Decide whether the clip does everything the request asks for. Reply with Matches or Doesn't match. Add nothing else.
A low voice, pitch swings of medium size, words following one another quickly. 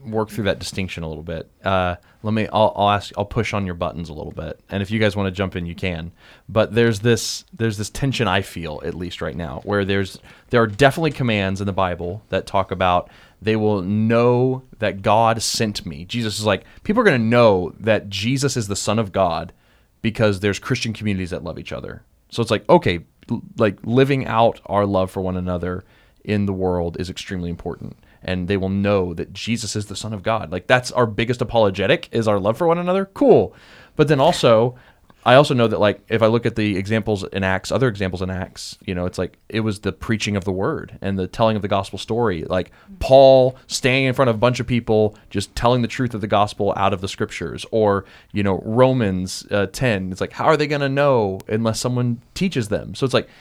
Matches